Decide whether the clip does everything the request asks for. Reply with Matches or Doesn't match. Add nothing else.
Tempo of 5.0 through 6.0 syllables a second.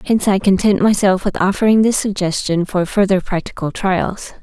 Matches